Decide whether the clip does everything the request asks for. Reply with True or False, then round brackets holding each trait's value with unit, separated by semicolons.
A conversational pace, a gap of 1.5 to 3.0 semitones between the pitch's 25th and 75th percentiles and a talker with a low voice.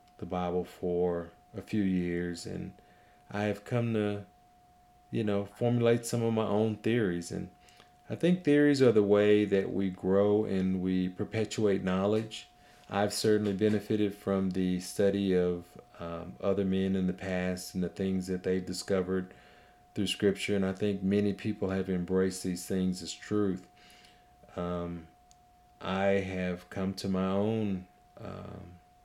True (150 wpm; 2.4 semitones; 95 Hz)